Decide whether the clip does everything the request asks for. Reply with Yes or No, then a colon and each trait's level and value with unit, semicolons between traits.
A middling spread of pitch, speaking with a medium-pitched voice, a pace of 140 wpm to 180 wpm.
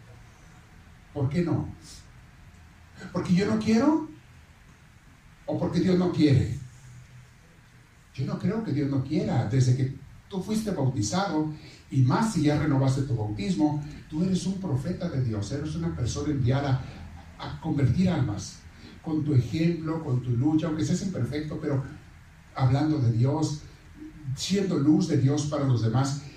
Yes: average, 4.3 semitones; medium, 145 Hz; average, 145 wpm